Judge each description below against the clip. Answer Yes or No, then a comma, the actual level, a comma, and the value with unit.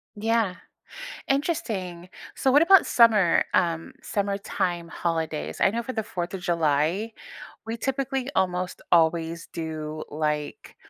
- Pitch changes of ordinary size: No, wide, 5.7 semitones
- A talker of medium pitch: Yes, medium, 180 Hz